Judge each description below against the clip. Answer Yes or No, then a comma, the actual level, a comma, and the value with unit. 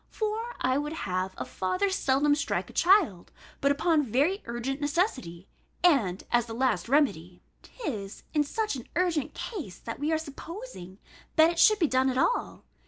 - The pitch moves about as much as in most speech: No, wide, 6.7 semitones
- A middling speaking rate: Yes, average, 170 wpm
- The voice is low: No, very high, 285 Hz